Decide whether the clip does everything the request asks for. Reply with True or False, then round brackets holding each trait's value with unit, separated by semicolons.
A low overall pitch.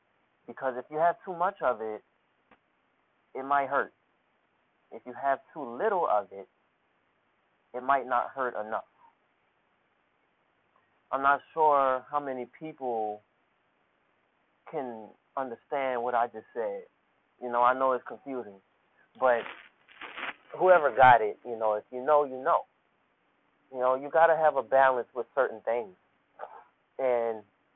True (130 Hz)